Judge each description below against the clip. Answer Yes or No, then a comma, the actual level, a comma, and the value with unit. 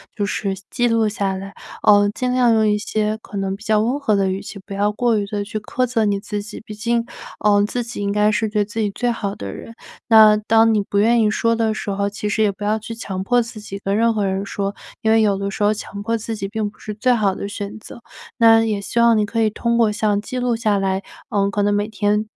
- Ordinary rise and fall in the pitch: No, narrow, 1.9 semitones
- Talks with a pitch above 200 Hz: Yes, high, 210 Hz